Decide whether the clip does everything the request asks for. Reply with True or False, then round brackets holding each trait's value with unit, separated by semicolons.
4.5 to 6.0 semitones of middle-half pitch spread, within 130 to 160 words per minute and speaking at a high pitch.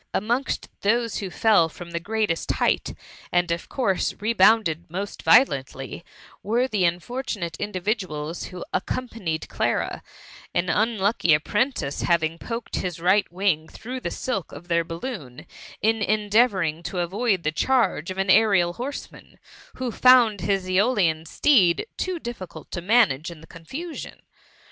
True (5.2 semitones; 140 wpm; 195 Hz)